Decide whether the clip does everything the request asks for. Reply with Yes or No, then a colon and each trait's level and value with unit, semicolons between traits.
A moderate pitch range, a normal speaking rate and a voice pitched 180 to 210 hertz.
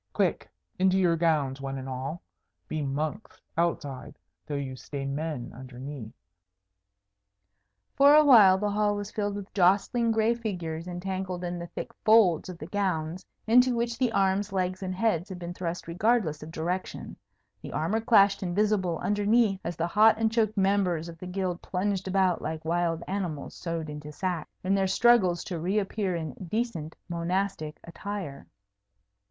Yes: average, 4.1 semitones; average, 160 wpm; medium, 185 Hz